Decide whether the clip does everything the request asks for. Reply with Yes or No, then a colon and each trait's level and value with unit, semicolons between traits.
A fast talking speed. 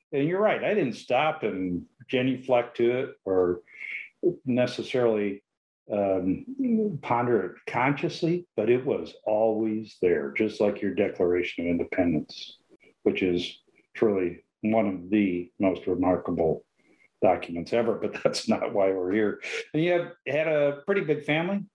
No: average, 140 wpm